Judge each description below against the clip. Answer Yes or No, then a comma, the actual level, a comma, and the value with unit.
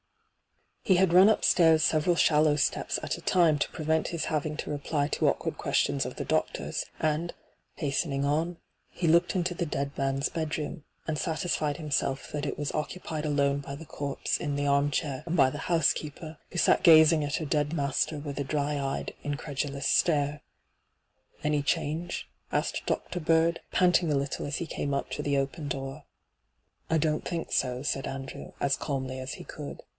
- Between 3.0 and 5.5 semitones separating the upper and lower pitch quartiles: No, narrow, 2.4 semitones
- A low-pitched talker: No, medium, 150 Hz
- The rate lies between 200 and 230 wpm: No, average, 185 wpm